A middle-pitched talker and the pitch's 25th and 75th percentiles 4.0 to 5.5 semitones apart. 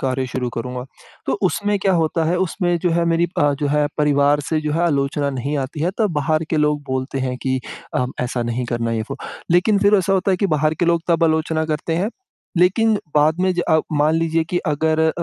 No: medium, 155 Hz; average, 3.6 semitones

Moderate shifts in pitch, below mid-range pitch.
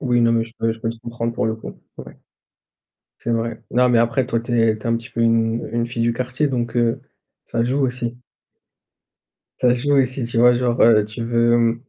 No: narrow, 1.1 semitones; low, 120 Hz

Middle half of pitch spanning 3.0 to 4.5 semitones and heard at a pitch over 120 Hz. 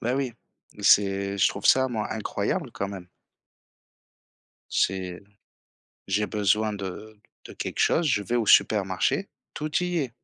No: average, 3.8 semitones; low, 105 Hz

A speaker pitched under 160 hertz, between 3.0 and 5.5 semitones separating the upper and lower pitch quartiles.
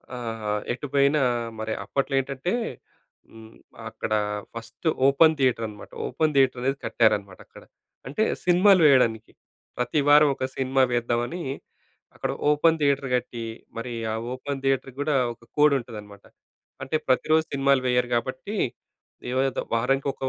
Yes: low, 135 Hz; average, 3.4 semitones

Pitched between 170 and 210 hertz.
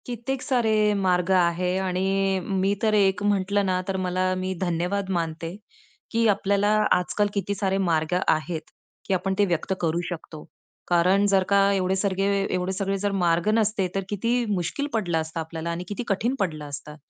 Yes: high, 190 Hz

